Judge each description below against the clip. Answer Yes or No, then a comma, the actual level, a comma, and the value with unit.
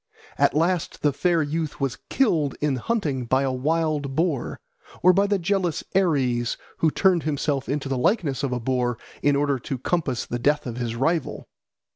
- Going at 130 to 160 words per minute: No, average, 180 wpm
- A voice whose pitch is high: No, medium, 145 Hz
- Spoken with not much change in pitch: No, average, 4.2 semitones